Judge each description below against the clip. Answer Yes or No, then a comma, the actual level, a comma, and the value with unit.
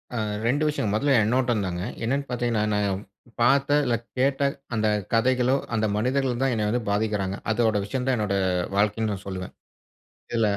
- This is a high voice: No, low, 115 Hz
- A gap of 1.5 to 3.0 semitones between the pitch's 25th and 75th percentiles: No, average, 3.7 semitones